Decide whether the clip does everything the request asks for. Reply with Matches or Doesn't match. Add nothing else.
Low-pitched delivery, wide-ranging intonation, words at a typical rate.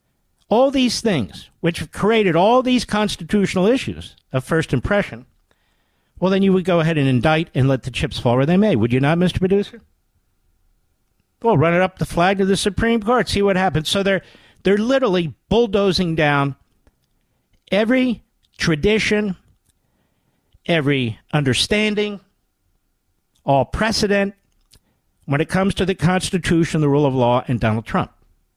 Doesn't match